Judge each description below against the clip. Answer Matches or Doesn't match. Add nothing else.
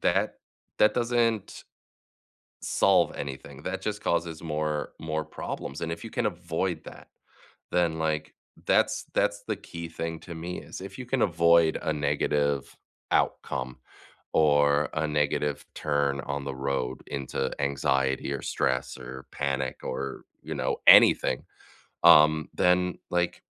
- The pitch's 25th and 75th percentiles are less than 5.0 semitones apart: Matches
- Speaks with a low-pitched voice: Matches